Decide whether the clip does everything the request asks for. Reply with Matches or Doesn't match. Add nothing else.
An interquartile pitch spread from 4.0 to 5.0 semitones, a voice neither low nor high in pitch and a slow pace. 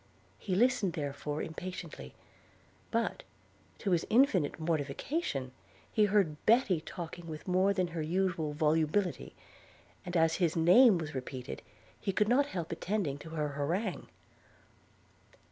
Matches